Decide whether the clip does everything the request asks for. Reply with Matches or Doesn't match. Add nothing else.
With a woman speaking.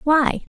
Matches